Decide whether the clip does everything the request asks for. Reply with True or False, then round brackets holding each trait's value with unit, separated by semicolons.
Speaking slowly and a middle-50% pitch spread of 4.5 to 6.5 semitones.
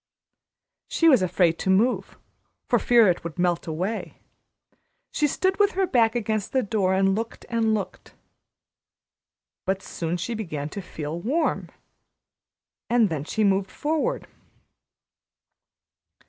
True (130 wpm; 5.1 semitones)